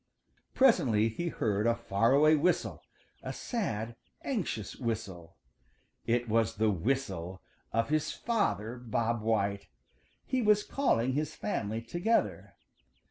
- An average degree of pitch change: No, wide, 6.6 semitones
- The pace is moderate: No, slow, 120 wpm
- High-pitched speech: No, low, 115 Hz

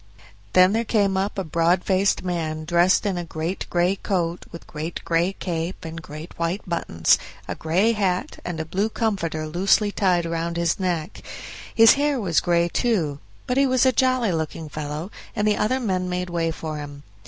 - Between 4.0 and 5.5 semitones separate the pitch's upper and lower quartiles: No, average, 3.5 semitones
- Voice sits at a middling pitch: Yes, medium, 175 Hz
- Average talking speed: Yes, average, 190 wpm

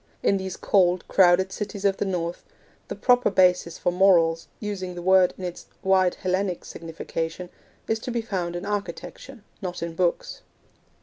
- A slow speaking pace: No, average, 165 wpm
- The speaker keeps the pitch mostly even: Yes, narrow, 2.1 semitones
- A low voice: No, medium, 185 Hz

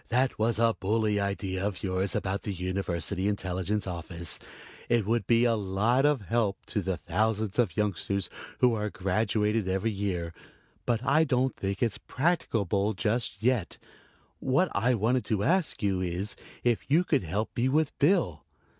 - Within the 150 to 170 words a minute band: Yes, average, 165 wpm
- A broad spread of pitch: No, average, 3.8 semitones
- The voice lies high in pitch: No, low, 105 Hz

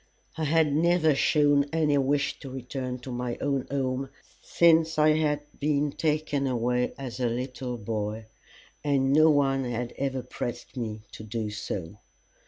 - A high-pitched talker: No, low, 135 Hz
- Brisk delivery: No, average, 155 wpm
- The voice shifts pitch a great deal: No, average, 3.2 semitones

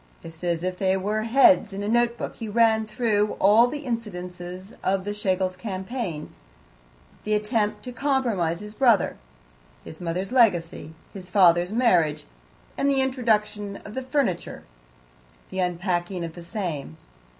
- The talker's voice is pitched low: No, high, 205 Hz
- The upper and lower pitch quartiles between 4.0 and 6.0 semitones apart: Yes, average, 4.5 semitones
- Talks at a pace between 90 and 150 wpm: Yes, average, 140 wpm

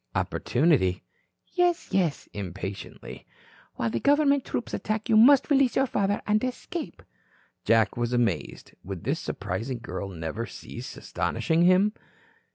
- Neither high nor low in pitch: Yes, medium, 170 Hz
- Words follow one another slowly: Yes, slow, 130 wpm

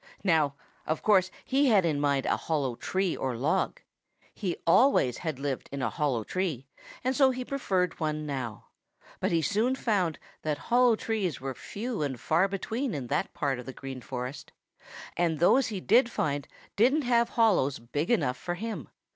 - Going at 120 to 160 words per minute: No, average, 180 wpm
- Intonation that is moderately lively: No, wide, 8.1 semitones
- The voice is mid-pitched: Yes, medium, 170 Hz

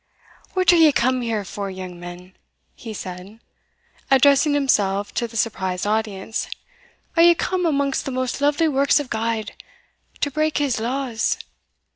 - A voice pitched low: No, high, 235 Hz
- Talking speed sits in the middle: Yes, average, 150 wpm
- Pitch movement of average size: No, wide, 5.9 semitones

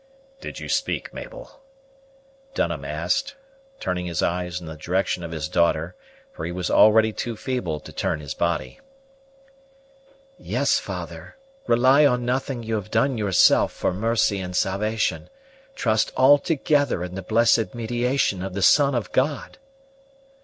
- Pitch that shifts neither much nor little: No, wide, 6.1 semitones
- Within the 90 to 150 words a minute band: Yes, average, 145 wpm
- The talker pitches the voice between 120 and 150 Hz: No, low, 110 Hz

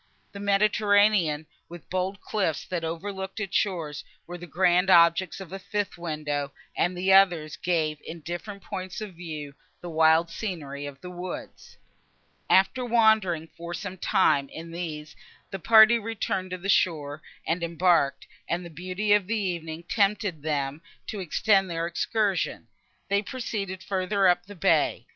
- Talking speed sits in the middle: Yes, average, 155 wpm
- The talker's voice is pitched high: No, medium, 180 Hz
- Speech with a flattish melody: No, average, 3.4 semitones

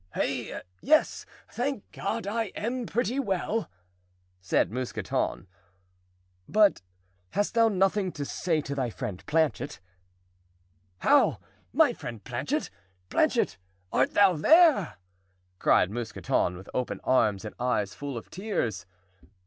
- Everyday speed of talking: No, slow, 115 wpm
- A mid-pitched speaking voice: Yes, medium, 155 Hz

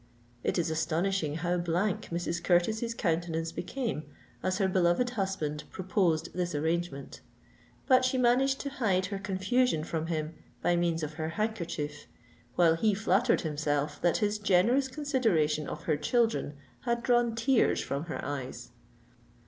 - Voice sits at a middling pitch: Yes, medium, 180 Hz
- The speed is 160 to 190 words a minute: No, average, 145 wpm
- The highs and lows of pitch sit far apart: Yes, wide, 5.8 semitones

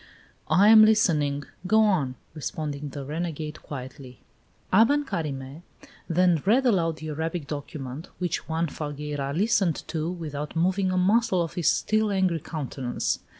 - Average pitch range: Yes, average, 4.3 semitones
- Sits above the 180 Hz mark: No, medium, 165 Hz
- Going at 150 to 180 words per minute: No, average, 140 wpm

